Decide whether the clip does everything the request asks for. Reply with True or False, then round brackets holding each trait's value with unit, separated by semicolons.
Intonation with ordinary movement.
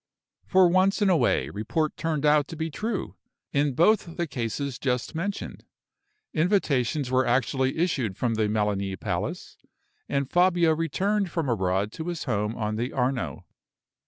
False (6.5 semitones)